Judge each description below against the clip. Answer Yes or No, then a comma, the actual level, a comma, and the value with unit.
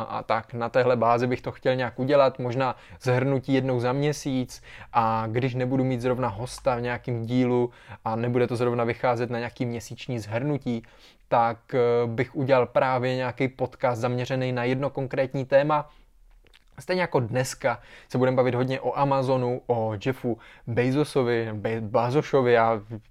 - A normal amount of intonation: No, narrow, 1.8 semitones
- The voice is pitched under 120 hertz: No, low, 125 Hz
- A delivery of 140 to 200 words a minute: Yes, average, 150 wpm